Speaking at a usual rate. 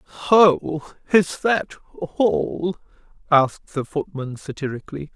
No: slow, 95 wpm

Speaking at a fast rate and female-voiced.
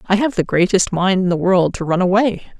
Yes: fast, 255 wpm; female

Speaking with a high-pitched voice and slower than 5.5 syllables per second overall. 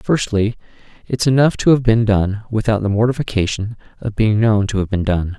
No: low, 110 Hz; 5.3 syllables/s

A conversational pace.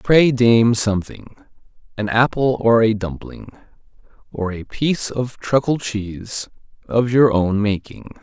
No: slow, 130 wpm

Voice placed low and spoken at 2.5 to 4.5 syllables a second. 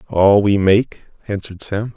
Yes: low, 100 Hz; 4.4 syllables/s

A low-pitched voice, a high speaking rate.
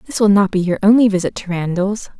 No: high, 200 Hz; fast, 245 wpm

